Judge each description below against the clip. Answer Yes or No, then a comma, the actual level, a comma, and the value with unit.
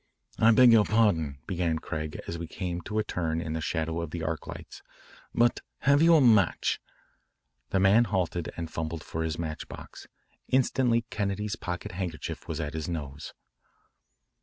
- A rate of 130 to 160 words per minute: No, average, 170 wpm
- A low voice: Yes, very low, 85 Hz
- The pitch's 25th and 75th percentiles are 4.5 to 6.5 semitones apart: Yes, average, 4.9 semitones